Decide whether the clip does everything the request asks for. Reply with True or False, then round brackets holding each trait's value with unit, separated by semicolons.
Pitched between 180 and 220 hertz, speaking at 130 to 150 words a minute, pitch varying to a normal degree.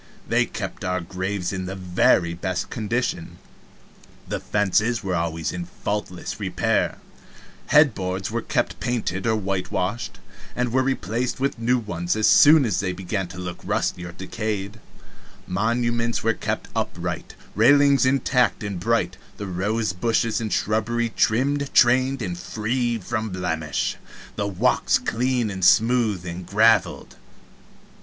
False (105 Hz; 140 wpm; 4.4 semitones)